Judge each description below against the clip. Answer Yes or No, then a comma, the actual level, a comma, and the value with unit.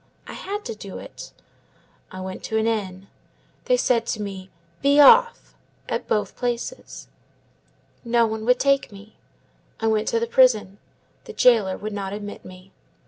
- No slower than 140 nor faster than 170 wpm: Yes, average, 160 wpm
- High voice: Yes, high, 220 Hz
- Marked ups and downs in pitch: No, average, 4.0 semitones